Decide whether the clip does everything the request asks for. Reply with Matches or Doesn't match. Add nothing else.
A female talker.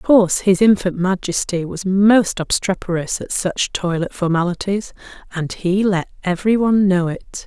Matches